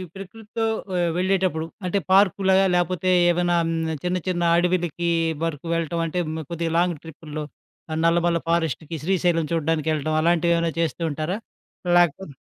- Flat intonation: Yes, narrow, 1.9 semitones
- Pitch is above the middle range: No, medium, 170 Hz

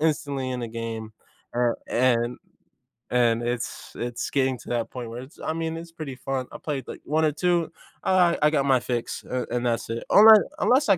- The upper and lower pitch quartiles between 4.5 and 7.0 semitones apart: Yes, average, 4.9 semitones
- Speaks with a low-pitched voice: Yes, low, 130 Hz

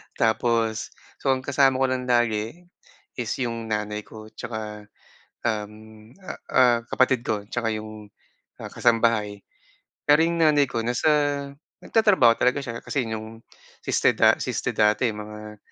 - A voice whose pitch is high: No, low, 115 Hz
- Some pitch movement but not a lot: Yes, average, 3.3 semitones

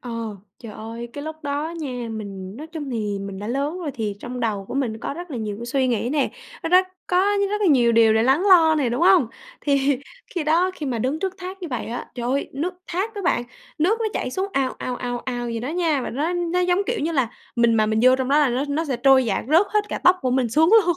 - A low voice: No, very high, 275 Hz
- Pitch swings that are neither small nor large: No, wide, 5.8 semitones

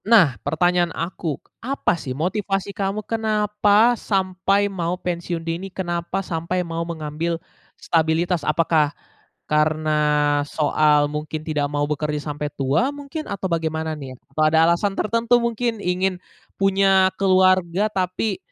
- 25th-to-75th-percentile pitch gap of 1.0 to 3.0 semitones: No, average, 4.0 semitones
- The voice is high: No, medium, 175 Hz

